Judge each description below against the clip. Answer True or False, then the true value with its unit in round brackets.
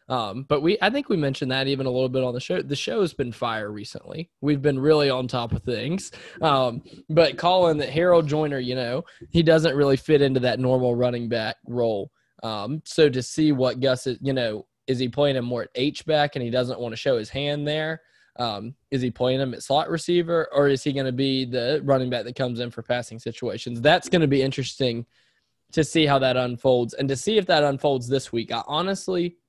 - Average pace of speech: False (230 wpm)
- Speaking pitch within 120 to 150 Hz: True (135 Hz)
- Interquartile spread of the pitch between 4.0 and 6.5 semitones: False (3.6 semitones)